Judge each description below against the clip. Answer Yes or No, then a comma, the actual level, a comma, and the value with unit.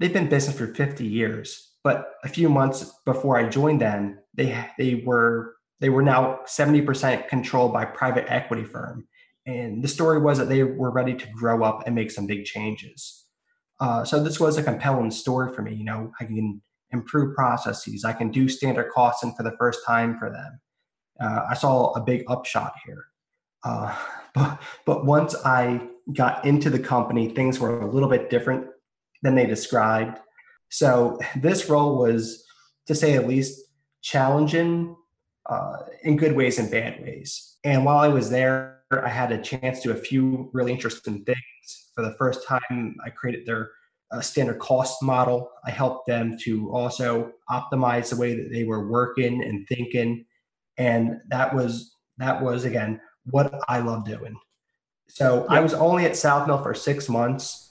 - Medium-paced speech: Yes, average, 180 wpm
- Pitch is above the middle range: No, low, 125 Hz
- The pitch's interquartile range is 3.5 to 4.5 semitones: No, average, 2.7 semitones